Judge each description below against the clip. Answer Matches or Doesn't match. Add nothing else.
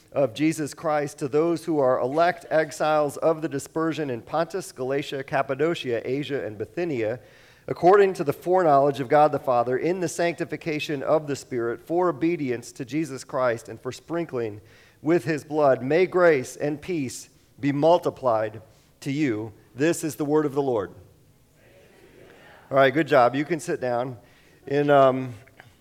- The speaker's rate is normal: Matches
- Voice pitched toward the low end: Doesn't match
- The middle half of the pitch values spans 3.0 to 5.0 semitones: Matches